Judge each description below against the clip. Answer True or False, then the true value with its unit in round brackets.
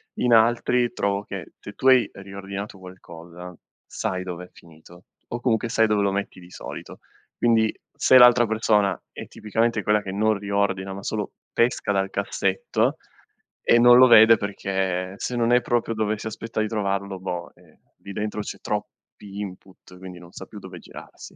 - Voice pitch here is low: True (100 Hz)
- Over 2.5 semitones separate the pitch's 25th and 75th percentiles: True (2.9 semitones)